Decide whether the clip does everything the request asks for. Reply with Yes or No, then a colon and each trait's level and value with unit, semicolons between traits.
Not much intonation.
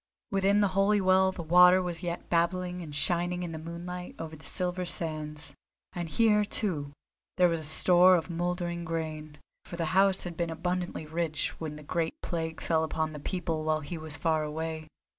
Yes: narrow, 2.2 semitones